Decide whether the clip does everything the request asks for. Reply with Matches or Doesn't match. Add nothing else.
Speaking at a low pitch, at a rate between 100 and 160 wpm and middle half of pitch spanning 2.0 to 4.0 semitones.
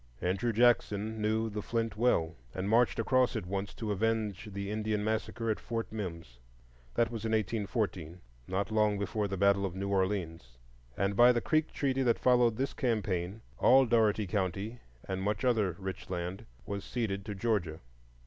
Doesn't match